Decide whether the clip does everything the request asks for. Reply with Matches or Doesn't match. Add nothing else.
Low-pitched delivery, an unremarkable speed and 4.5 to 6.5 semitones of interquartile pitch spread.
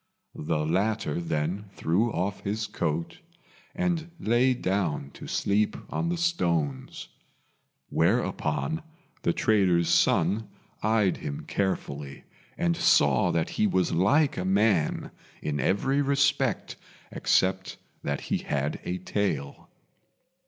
Doesn't match